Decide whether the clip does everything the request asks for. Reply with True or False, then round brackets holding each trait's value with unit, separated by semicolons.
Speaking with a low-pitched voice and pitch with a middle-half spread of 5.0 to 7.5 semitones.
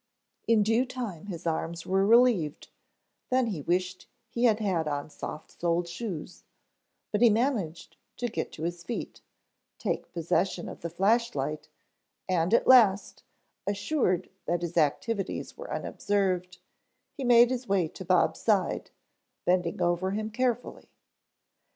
False (190 Hz; 5.3 semitones)